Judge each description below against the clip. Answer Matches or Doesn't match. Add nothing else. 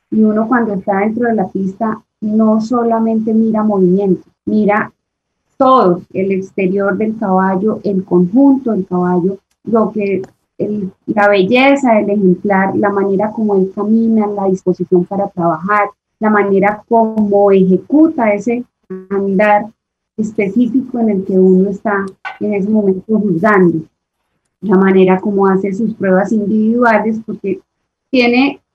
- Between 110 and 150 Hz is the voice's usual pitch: Doesn't match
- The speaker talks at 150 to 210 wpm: Doesn't match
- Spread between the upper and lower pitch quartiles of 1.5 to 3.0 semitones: Matches